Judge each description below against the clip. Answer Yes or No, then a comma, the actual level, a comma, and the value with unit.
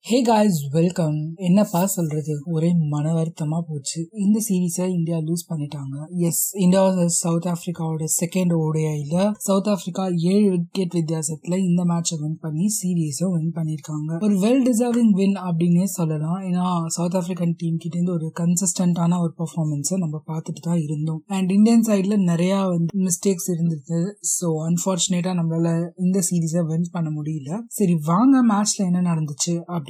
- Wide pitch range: No, narrow, 2.4 semitones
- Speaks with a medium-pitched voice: Yes, medium, 175 Hz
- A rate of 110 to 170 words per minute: Yes, average, 120 wpm